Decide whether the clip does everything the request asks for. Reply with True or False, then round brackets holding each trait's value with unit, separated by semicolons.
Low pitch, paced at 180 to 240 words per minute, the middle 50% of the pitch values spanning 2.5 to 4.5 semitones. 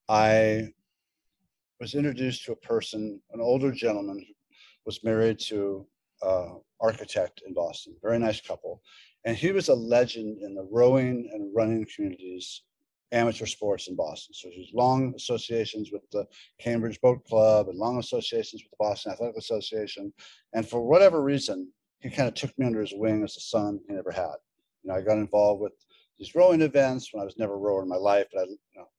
True (110 Hz; 190 wpm; 3.6 semitones)